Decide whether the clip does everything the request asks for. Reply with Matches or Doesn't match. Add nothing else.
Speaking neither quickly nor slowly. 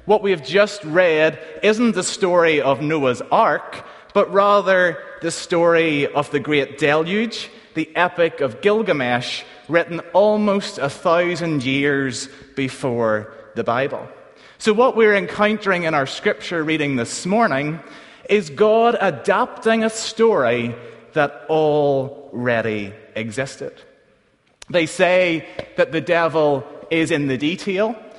Doesn't match